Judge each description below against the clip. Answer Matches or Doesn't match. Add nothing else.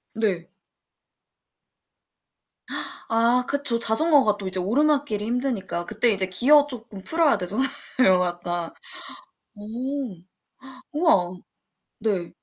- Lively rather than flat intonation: Matches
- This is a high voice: Matches